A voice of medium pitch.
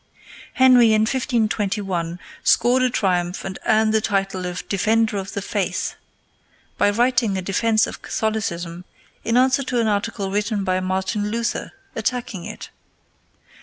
No: high, 215 Hz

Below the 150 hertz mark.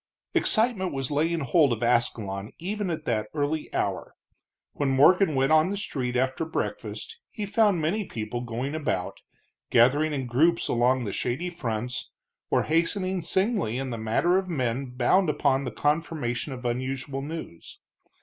Yes: medium, 140 Hz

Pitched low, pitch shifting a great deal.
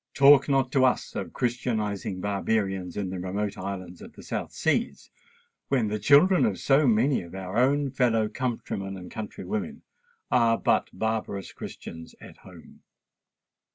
No: low, 110 Hz; average, 4.9 semitones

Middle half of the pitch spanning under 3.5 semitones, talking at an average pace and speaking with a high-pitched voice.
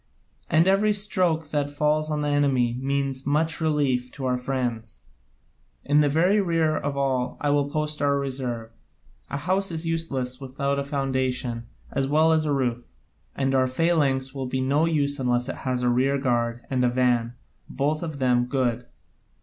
No: average, 3.1 semitones; average, 180 wpm; medium, 140 Hz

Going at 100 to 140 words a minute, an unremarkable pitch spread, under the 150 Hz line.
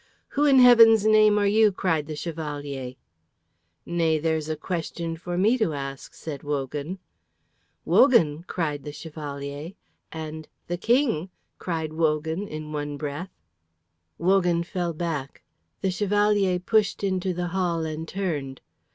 No: slow, 135 wpm; average, 4.2 semitones; medium, 165 Hz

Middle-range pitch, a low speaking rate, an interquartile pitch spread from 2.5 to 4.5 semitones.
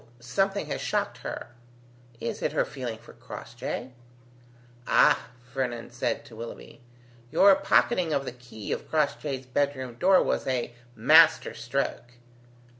No: low, 130 Hz; slow, 130 wpm; average, 3.8 semitones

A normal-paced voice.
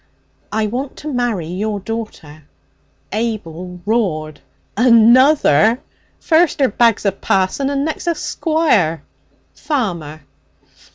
No: slow, 105 wpm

